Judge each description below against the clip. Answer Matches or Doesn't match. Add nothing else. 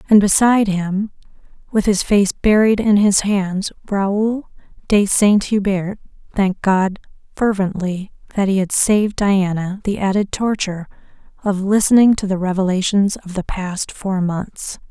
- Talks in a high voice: Matches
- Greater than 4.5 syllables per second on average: Doesn't match